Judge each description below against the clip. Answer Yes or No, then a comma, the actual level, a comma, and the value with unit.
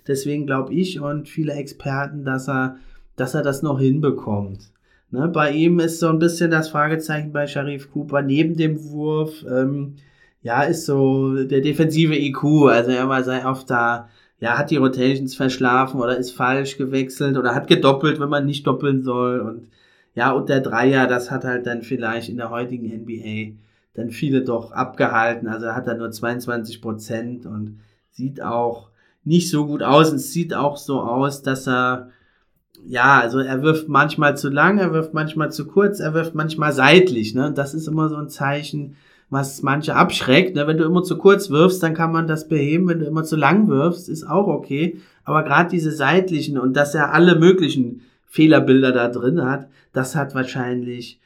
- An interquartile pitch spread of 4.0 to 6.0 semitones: No, average, 3.6 semitones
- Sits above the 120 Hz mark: Yes, medium, 140 Hz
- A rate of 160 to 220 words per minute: Yes, average, 185 wpm